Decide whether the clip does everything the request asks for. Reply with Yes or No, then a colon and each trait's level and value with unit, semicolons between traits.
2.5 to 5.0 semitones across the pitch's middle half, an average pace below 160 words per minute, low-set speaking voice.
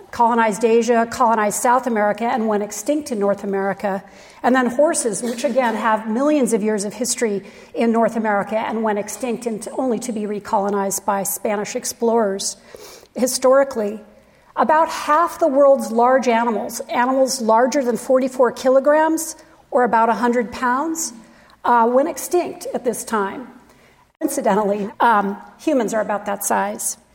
No: average, 3.8 semitones; average, 145 wpm; high, 235 Hz